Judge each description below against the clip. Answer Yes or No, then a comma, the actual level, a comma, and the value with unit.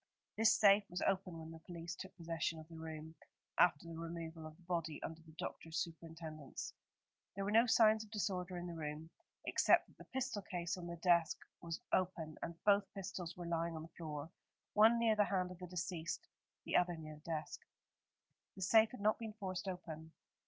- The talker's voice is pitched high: No, medium, 170 Hz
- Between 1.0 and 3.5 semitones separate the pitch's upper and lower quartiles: Yes, average, 3.2 semitones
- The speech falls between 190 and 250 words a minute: Yes, average, 200 wpm